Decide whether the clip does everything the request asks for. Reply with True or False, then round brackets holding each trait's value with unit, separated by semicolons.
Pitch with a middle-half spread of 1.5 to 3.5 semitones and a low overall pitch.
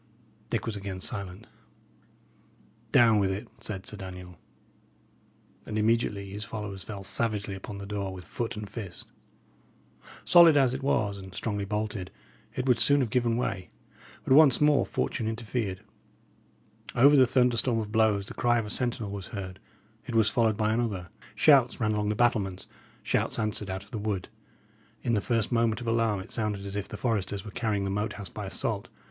True (2.9 semitones; 105 Hz)